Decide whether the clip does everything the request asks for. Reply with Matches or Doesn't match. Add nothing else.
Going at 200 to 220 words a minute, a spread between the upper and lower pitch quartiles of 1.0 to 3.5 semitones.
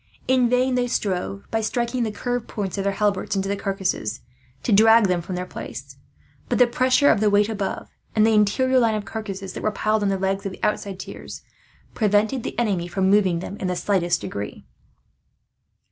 Matches